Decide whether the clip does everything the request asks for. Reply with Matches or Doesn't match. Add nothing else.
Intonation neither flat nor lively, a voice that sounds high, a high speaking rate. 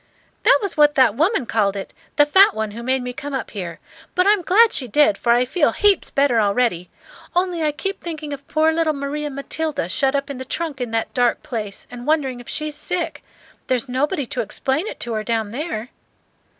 Matches